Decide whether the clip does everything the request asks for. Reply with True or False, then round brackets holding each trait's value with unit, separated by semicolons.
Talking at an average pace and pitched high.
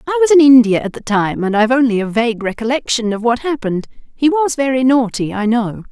False (225 wpm; 240 Hz)